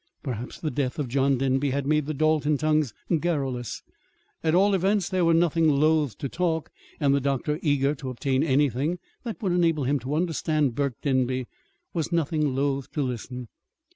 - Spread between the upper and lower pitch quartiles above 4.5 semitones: No, average, 3.1 semitones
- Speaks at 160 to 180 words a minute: Yes, average, 175 wpm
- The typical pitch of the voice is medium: Yes, medium, 145 Hz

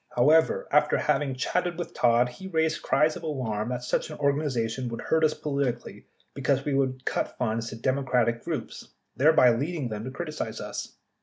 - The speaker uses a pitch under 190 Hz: Yes, low, 135 Hz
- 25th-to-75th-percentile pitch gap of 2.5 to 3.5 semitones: No, average, 3.9 semitones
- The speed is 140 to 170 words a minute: No, average, 180 wpm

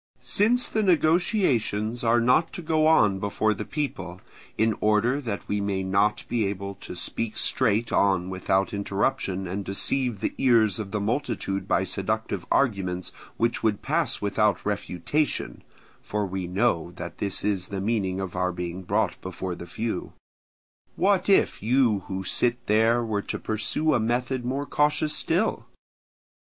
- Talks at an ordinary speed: Yes, average, 155 wpm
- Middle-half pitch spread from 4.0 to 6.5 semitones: Yes, average, 4.6 semitones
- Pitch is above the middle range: No, low, 105 Hz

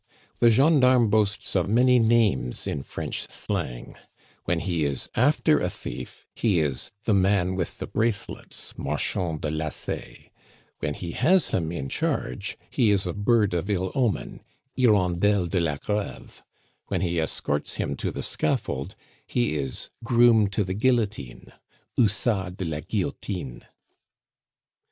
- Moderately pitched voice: No, very low, 95 Hz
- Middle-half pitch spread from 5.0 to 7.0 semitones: Yes, wide, 5.5 semitones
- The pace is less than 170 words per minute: Yes, average, 140 wpm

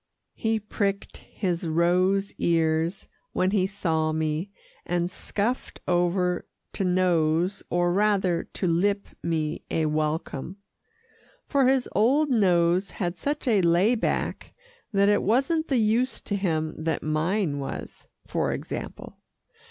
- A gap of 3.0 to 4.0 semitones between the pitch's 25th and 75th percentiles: Yes, average, 3.7 semitones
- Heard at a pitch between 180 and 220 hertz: Yes, medium, 185 Hz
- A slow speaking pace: Yes, slow, 130 wpm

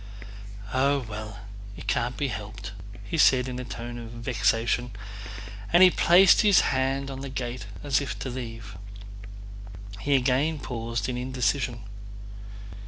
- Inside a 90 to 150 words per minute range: Yes, slow, 135 wpm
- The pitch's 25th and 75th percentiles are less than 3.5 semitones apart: Yes, average, 2.8 semitones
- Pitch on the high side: No, low, 125 Hz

